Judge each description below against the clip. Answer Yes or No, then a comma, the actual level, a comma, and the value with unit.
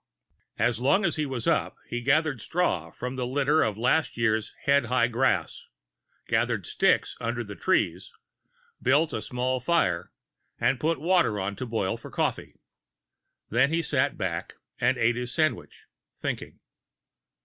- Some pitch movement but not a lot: Yes, average, 4.4 semitones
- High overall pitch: No, low, 125 Hz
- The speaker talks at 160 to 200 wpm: No, average, 150 wpm